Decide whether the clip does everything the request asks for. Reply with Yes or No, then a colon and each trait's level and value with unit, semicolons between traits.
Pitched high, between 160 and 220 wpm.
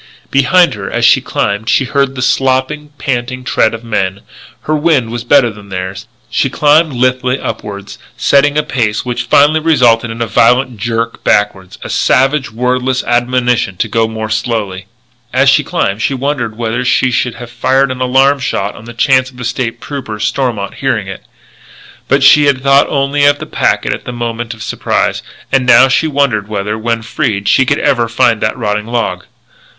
No: low, 120 Hz; average, 185 wpm